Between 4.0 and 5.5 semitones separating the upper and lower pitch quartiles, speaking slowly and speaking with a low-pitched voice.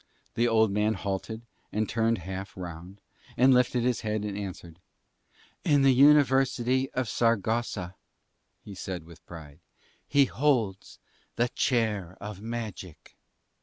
Yes: average, 4.3 semitones; slow, 130 wpm; low, 110 Hz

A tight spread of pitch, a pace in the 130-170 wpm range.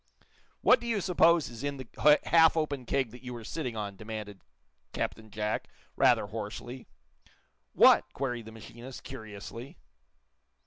No: average, 4.6 semitones; average, 140 wpm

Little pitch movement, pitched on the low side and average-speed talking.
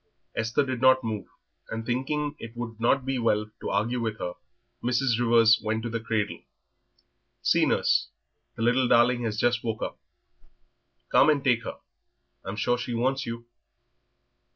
Yes: narrow, 2.1 semitones; low, 120 Hz; average, 170 wpm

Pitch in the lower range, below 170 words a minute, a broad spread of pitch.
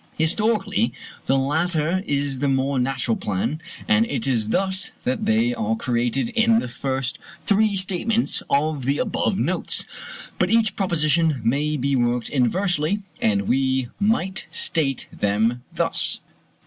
No: medium, 150 Hz; average, 140 wpm; wide, 7.4 semitones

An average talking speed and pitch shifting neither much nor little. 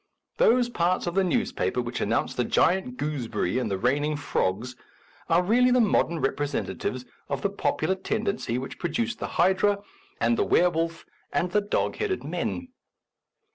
No: average, 160 wpm; wide, 8.1 semitones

